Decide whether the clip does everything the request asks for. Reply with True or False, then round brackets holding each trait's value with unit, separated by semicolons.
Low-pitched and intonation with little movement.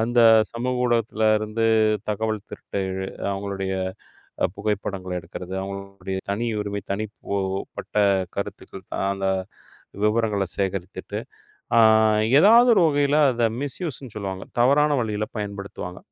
False (105 Hz; 3.3 semitones)